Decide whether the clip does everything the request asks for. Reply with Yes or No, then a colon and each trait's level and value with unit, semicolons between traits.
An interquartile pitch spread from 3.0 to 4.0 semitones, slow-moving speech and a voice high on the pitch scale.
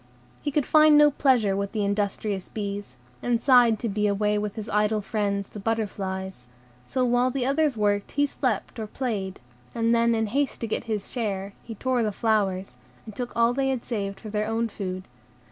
No: average, 3.3 semitones; average, 195 wpm; high, 220 Hz